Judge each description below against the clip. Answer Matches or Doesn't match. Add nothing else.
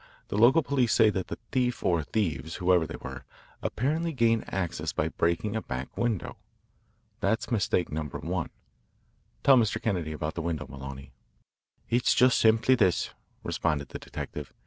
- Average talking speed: Matches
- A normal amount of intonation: Doesn't match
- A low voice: Matches